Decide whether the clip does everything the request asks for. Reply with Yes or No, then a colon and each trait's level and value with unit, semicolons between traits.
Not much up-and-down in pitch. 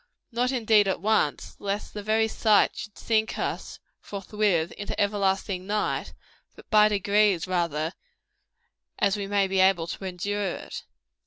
Yes: narrow, 2.1 semitones